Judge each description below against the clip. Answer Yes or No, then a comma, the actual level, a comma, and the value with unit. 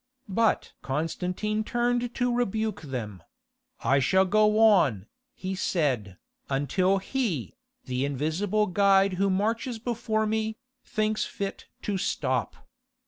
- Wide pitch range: Yes, wide, 6.2 semitones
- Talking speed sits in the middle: No, slow, 115 wpm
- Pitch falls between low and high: No, high, 195 Hz